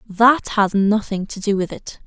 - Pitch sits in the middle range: No, high, 205 Hz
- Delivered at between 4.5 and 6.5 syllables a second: No, 4.1 syllables/s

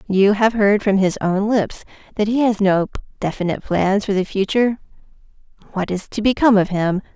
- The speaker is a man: No, female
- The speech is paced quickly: No, average, 185 wpm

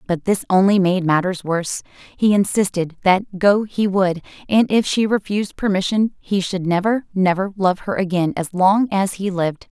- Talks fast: No, average, 180 wpm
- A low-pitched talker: No, high, 190 Hz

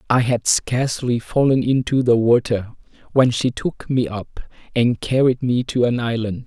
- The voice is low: Yes, low, 120 Hz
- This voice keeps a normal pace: Yes, average, 165 wpm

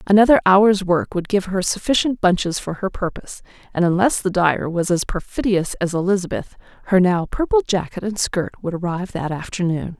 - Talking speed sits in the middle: Yes, average, 180 wpm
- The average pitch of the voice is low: No, high, 190 Hz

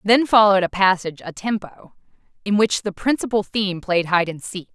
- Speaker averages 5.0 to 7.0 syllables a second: Yes, 5.7 syllables/s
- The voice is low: No, high, 195 Hz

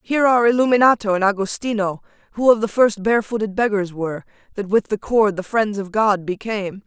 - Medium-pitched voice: No, high, 210 Hz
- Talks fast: No, average, 185 wpm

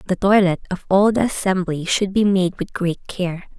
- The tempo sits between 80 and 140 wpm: No, average, 200 wpm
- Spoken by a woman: Yes, female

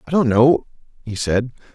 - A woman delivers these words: No, male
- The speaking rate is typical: Yes, average, 170 wpm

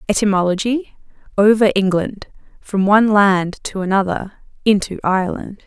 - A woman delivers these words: Yes, female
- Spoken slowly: Yes, slow, 105 wpm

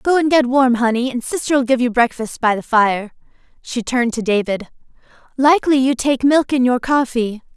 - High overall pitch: Yes, very high, 250 Hz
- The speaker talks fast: No, average, 190 wpm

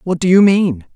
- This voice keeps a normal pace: No, fast, 250 wpm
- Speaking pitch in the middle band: Yes, medium, 180 Hz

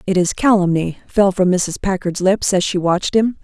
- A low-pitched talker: No, high, 190 Hz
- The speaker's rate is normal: No, fast, 210 wpm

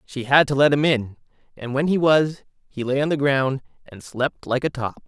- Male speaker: Yes, male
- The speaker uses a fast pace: Yes, fast, 235 wpm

